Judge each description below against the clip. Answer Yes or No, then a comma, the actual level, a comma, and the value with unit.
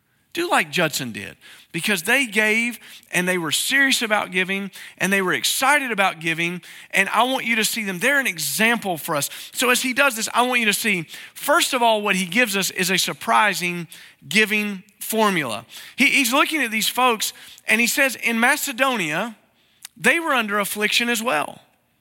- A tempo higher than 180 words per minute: Yes, average, 190 wpm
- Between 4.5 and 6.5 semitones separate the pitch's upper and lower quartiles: Yes, average, 5.1 semitones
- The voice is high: Yes, high, 215 Hz